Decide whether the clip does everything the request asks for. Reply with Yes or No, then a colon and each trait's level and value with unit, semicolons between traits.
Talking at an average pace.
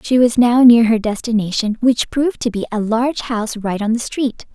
No: fast, 225 wpm